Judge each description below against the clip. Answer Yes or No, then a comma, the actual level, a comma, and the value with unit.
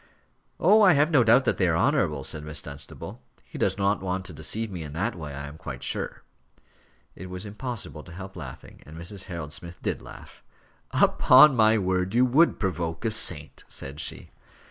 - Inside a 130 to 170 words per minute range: No, average, 195 wpm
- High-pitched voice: No, very low, 90 Hz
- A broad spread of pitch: Yes, wide, 6.4 semitones